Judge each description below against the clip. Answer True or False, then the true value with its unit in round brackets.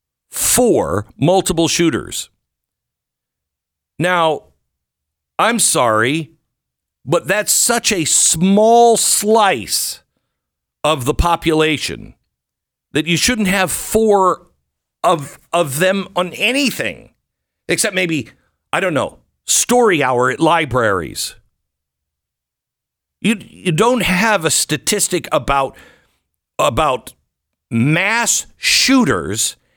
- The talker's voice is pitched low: False (165 Hz)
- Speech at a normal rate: False (90 wpm)